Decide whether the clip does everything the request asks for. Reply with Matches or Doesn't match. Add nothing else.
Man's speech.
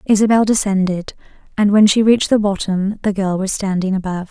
Doesn't match